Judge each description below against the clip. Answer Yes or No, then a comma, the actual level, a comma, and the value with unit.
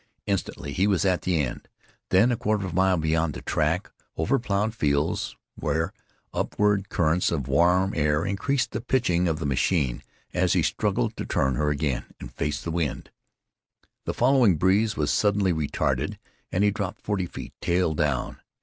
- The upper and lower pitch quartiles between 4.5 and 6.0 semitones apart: Yes, average, 5.0 semitones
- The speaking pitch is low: Yes, very low, 90 Hz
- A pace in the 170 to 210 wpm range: Yes, average, 175 wpm